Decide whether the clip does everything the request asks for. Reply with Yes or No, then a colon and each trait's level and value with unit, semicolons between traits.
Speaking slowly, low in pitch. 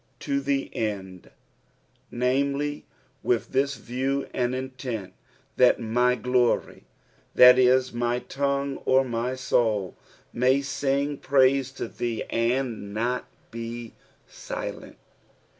Yes: slow, 125 wpm; low, 125 Hz